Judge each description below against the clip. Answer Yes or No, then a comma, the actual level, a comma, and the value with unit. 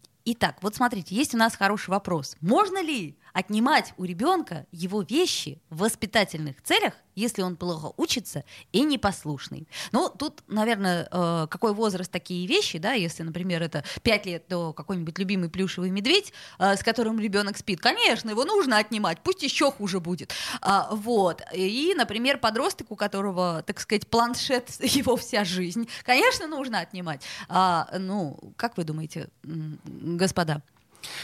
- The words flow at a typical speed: Yes, average, 140 wpm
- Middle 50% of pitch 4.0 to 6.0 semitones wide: Yes, average, 5.2 semitones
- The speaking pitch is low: No, high, 200 Hz